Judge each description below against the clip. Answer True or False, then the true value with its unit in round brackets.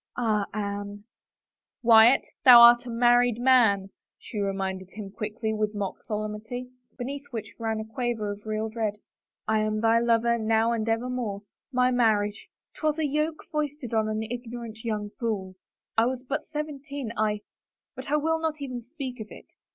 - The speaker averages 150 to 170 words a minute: False (190 wpm)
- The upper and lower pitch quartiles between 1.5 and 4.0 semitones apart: True (2.8 semitones)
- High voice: True (225 Hz)